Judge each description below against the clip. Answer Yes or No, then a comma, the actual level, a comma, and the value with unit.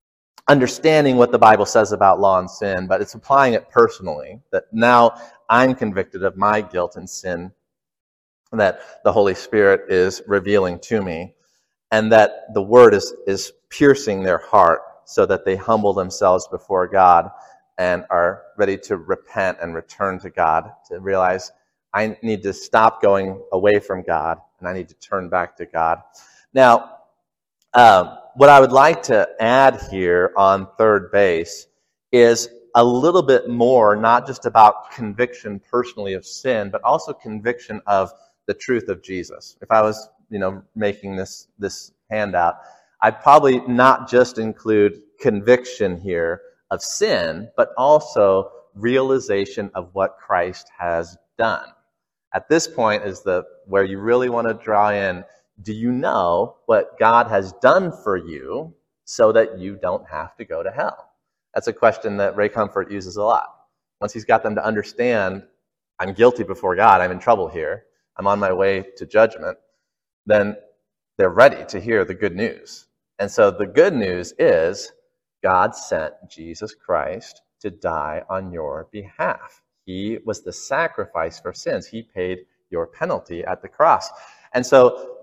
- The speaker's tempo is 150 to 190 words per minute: Yes, average, 160 wpm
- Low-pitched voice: Yes, low, 110 Hz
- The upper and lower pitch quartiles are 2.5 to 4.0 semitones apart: No, average, 5.2 semitones